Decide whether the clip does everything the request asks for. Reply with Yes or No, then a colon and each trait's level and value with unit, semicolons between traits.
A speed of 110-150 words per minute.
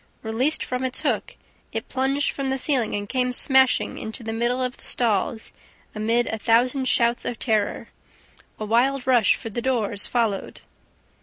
No: average, 165 wpm